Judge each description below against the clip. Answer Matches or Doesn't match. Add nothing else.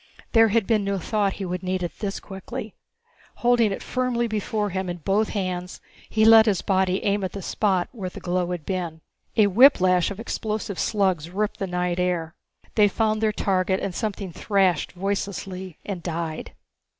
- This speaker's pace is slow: Doesn't match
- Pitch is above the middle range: Matches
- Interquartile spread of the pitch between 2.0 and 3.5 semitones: Matches